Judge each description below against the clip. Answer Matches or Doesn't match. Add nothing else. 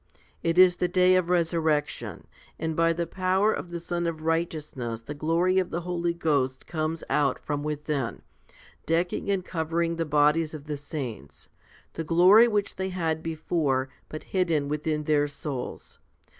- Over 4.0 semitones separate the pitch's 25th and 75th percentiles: Doesn't match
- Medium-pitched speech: Matches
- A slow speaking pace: Doesn't match